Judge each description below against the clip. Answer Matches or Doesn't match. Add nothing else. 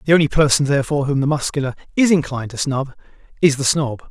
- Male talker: Matches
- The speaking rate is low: Doesn't match